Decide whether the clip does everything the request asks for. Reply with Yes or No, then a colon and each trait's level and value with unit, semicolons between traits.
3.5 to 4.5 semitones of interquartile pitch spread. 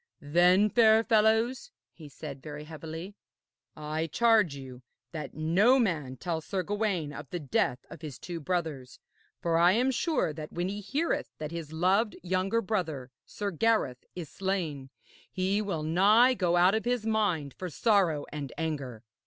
No: wide, 5.5 semitones